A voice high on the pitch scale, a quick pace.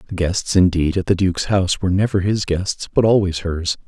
No: very low, 95 Hz; fast, 215 wpm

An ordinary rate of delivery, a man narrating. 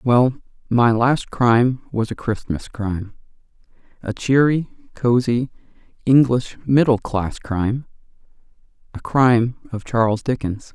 No: slow, 110 wpm; male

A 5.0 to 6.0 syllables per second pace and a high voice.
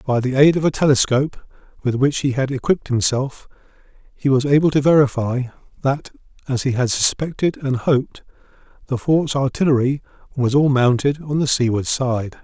No: 5.3 syllables/s; low, 135 Hz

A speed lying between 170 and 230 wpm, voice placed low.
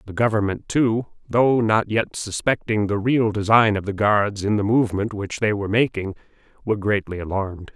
Yes: average, 180 wpm; low, 105 Hz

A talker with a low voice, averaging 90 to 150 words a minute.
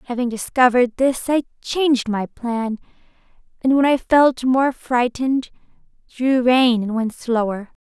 No: very high, 250 Hz; average, 140 wpm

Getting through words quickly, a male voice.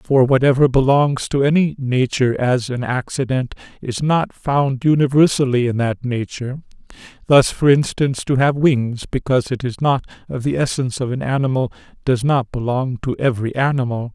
No: average, 160 wpm; male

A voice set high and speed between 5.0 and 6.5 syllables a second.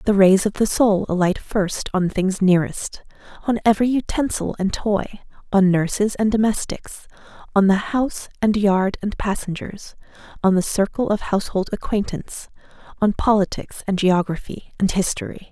Yes: high, 200 Hz; 5.1 syllables/s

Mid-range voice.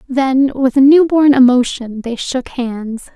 No: very high, 260 Hz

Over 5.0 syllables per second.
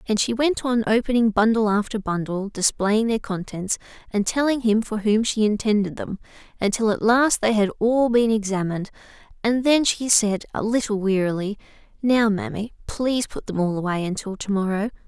Yes: 5.2 syllables/s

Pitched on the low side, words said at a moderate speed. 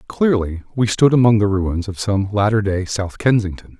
Yes: low, 105 Hz; average, 190 wpm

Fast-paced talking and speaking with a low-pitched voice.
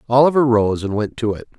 Yes: fast, 225 wpm; low, 115 Hz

